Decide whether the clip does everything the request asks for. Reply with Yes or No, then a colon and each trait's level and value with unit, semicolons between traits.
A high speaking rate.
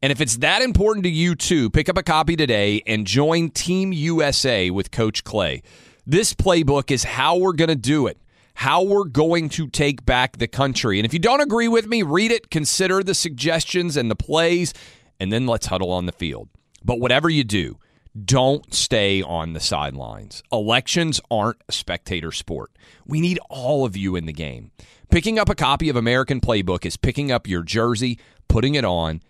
No: average, 195 wpm